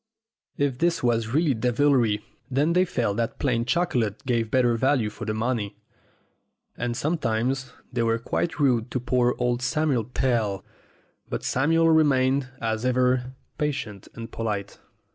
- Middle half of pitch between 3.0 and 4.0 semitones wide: Yes, average, 3.3 semitones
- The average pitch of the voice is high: No, low, 125 Hz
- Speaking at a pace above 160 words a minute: No, average, 145 wpm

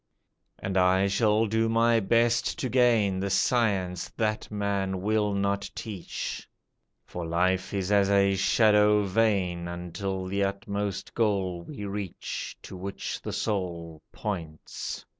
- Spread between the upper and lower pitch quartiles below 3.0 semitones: Yes, narrow, 2.4 semitones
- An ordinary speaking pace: No, slow, 130 wpm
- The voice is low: Yes, low, 100 Hz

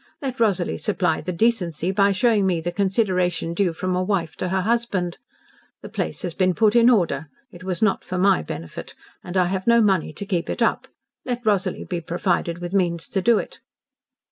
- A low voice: No, medium, 185 Hz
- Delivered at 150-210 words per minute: Yes, average, 200 wpm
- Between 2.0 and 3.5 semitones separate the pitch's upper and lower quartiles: Yes, average, 3.0 semitones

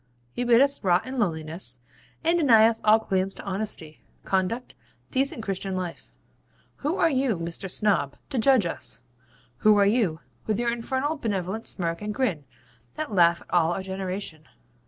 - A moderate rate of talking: Yes, average, 165 wpm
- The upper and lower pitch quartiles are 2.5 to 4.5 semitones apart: No, average, 5.3 semitones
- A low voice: No, high, 205 Hz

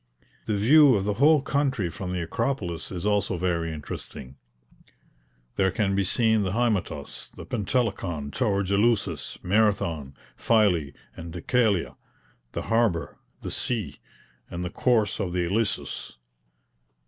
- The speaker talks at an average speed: No, slow, 130 wpm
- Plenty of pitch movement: No, average, 4.5 semitones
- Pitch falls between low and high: No, low, 100 Hz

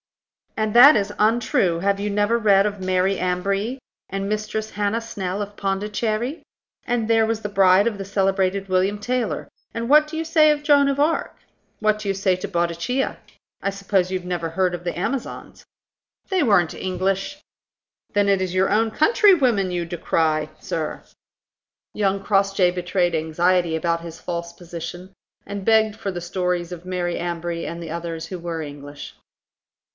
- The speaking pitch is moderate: No, high, 195 Hz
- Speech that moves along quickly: No, average, 170 wpm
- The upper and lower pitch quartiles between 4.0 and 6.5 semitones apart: No, average, 3.5 semitones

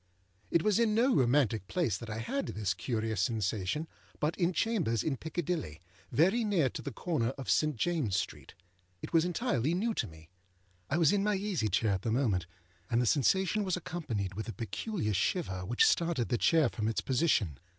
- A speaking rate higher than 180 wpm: Yes, average, 190 wpm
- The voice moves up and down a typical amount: No, wide, 8.1 semitones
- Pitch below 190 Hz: Yes, medium, 140 Hz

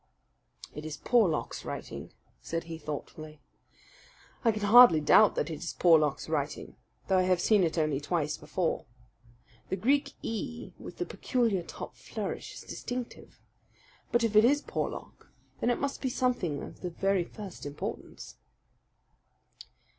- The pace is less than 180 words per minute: Yes, average, 145 wpm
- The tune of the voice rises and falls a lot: Yes, wide, 6.8 semitones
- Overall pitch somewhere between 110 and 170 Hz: No, medium, 185 Hz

